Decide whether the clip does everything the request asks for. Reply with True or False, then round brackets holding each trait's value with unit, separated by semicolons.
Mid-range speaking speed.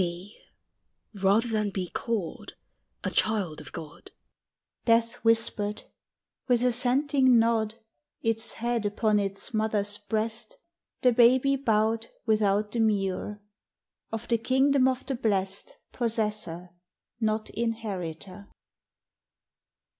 False (100 wpm)